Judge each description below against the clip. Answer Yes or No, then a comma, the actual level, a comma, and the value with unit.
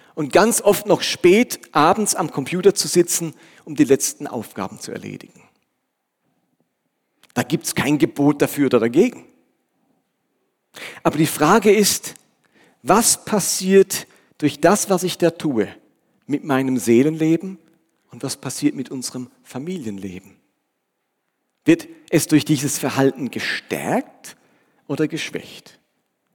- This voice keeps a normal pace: No, slow, 120 wpm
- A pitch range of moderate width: Yes, average, 4.8 semitones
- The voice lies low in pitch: No, medium, 155 Hz